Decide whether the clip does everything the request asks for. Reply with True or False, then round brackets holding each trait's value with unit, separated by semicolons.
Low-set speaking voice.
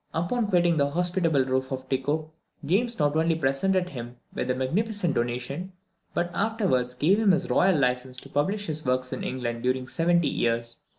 False (150 Hz)